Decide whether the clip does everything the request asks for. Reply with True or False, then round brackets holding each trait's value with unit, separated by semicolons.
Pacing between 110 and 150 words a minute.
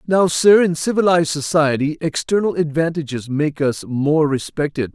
True (135 wpm)